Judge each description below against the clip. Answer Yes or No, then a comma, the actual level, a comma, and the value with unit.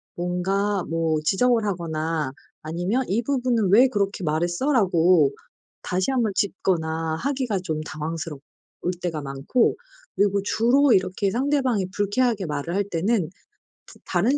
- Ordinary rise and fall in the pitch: No, wide, 5.8 semitones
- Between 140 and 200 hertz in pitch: Yes, high, 190 Hz